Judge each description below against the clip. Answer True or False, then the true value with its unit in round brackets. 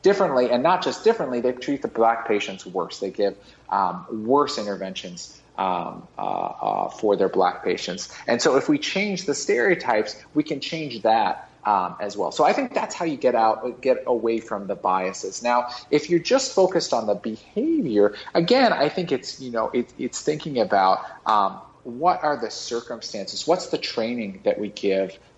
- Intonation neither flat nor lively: False (7.3 semitones)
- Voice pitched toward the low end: True (125 Hz)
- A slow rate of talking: False (185 wpm)